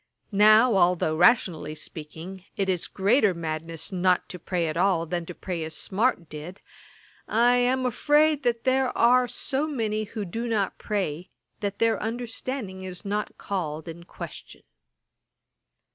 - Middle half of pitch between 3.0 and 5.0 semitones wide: No, wide, 5.5 semitones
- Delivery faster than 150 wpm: No, average, 145 wpm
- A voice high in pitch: Yes, high, 195 Hz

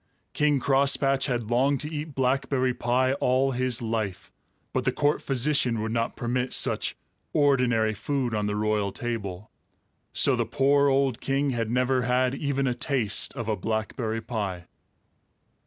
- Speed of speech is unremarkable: Yes, average, 155 wpm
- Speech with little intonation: No, average, 3.3 semitones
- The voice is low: Yes, low, 125 Hz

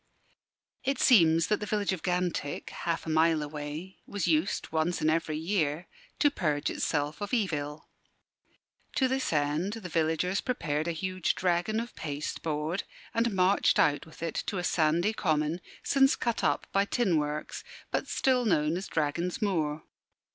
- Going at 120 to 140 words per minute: No, average, 160 wpm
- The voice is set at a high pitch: No, medium, 170 Hz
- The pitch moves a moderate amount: Yes, average, 4.6 semitones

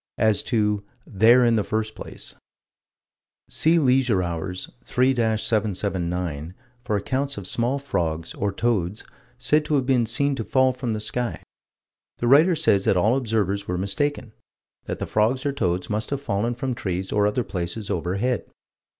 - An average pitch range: Yes, average, 4.7 semitones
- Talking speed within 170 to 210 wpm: No, average, 160 wpm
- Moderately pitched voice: No, low, 110 Hz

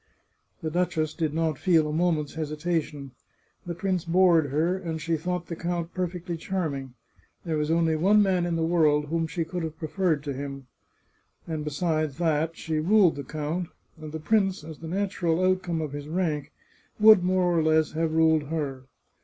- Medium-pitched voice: Yes, medium, 160 Hz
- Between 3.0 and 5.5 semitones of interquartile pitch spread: No, narrow, 2.5 semitones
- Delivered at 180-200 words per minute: Yes, average, 185 wpm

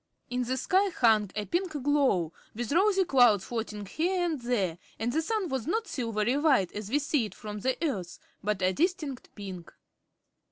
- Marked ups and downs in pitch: Yes, wide, 7.2 semitones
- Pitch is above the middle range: Yes, very high, 250 Hz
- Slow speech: No, average, 185 wpm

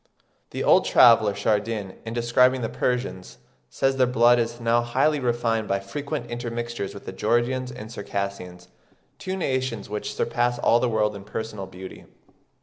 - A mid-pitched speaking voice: No, low, 115 Hz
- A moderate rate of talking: Yes, average, 155 wpm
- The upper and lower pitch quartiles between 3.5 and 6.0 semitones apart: No, average, 2.9 semitones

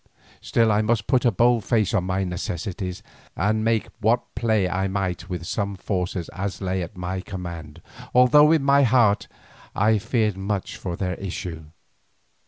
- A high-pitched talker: No, low, 100 Hz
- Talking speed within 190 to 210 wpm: No, average, 165 wpm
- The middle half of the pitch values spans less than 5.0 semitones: Yes, average, 3.6 semitones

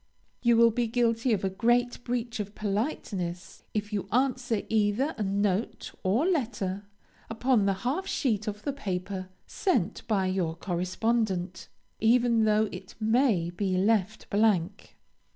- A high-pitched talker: Yes, high, 215 Hz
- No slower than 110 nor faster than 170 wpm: Yes, average, 140 wpm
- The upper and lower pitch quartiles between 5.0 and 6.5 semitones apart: No, average, 3.8 semitones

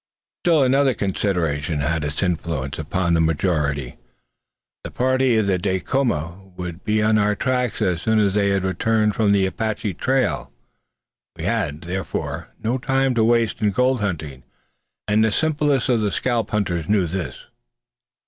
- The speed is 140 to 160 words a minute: Yes, average, 155 wpm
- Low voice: Yes, low, 100 Hz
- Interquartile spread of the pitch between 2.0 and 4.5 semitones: No, wide, 5.5 semitones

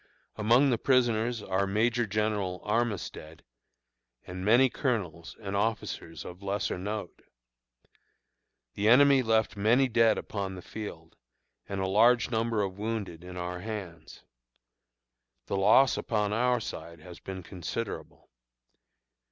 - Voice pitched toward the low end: Yes, low, 105 Hz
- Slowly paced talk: Yes, slow, 125 wpm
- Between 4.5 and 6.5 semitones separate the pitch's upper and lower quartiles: No, average, 3.7 semitones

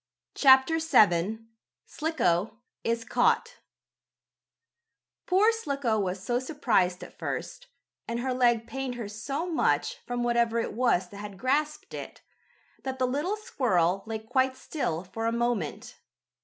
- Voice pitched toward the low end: No, high, 240 Hz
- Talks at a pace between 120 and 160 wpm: Yes, slow, 135 wpm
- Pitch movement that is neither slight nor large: Yes, average, 4.5 semitones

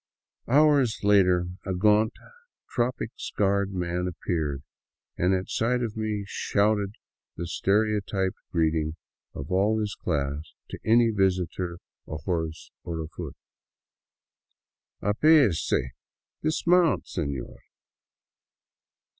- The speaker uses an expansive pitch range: No, average, 4.2 semitones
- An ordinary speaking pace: No, slow, 100 wpm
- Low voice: Yes, very low, 95 Hz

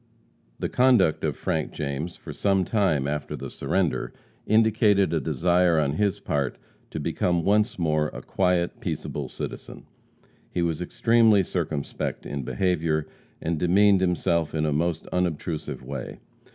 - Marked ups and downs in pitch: No, average, 4.0 semitones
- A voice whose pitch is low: Yes, very low, 85 Hz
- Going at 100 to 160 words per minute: Yes, average, 140 wpm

